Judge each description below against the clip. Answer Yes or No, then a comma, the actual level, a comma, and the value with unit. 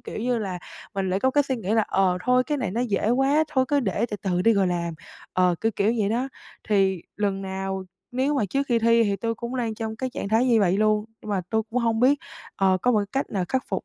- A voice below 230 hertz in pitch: Yes, high, 220 Hz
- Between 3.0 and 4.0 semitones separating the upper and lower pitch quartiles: No, average, 4.4 semitones